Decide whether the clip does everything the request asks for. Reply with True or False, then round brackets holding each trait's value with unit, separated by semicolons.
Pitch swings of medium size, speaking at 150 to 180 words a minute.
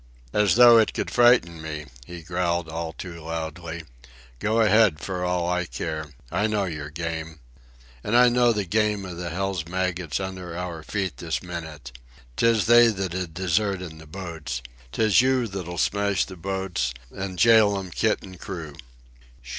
True (3.7 semitones; 165 wpm)